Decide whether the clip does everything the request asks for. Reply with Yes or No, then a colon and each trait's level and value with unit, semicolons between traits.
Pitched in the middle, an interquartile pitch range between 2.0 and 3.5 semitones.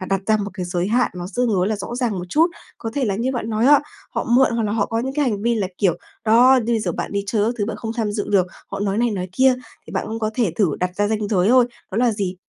No: high, 215 Hz; average, 3.1 semitones